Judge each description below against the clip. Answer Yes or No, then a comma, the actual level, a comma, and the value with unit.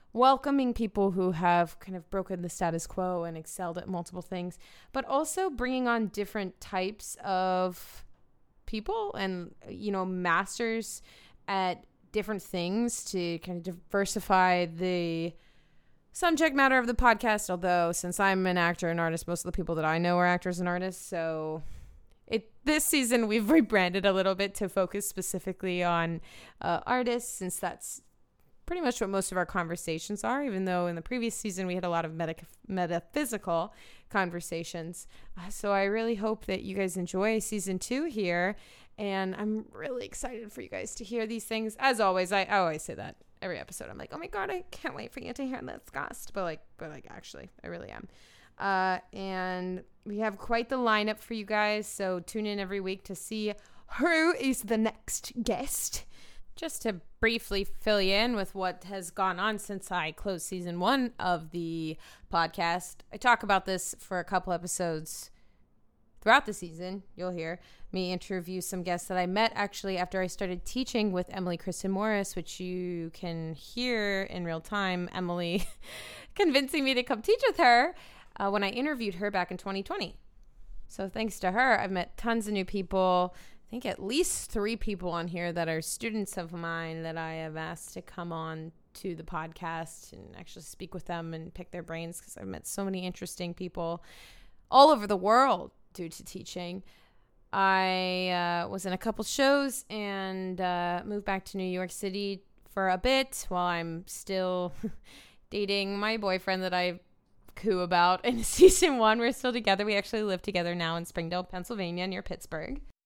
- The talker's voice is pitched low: No, high, 190 Hz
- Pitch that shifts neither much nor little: Yes, average, 3.6 semitones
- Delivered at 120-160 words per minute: No, average, 185 wpm